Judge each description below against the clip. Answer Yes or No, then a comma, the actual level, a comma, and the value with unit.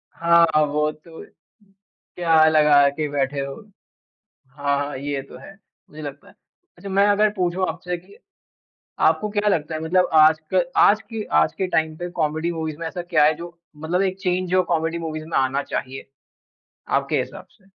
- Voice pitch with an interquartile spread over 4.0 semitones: No, average, 3.2 semitones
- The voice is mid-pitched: Yes, medium, 160 Hz